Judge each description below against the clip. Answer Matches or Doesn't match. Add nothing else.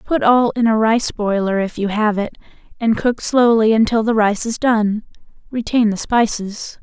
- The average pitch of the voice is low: Doesn't match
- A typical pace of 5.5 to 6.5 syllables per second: Doesn't match